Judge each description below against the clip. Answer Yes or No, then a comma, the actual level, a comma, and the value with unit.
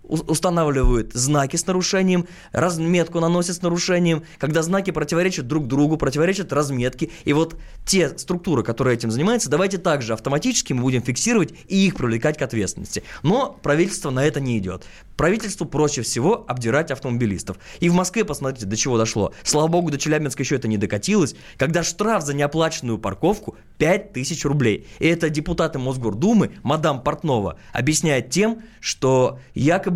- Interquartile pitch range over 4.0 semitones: Yes, average, 5.2 semitones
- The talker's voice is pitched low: No, medium, 150 Hz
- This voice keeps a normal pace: Yes, average, 150 wpm